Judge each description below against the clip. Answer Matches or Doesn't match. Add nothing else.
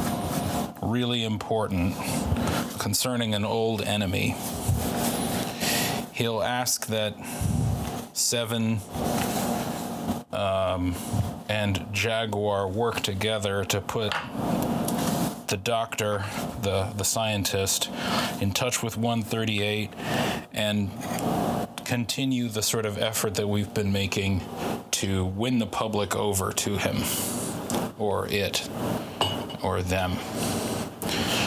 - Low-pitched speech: Matches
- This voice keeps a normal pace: Doesn't match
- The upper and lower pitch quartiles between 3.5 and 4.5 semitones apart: Doesn't match